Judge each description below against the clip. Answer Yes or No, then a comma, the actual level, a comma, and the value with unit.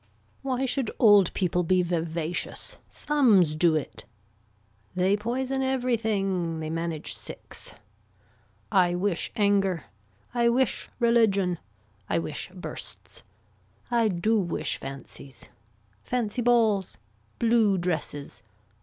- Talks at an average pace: No, slow, 100 wpm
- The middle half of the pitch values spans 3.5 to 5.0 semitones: No, wide, 5.4 semitones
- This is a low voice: No, high, 195 Hz